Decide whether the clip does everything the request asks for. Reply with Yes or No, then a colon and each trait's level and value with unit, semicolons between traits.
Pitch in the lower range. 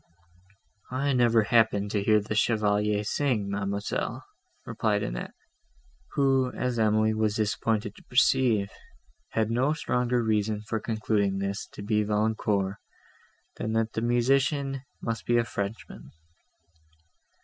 Yes: low, 110 Hz